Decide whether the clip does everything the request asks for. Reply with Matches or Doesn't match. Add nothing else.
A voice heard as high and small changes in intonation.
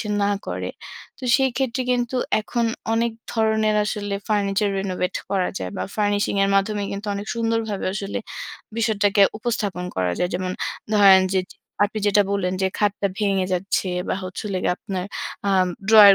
Matches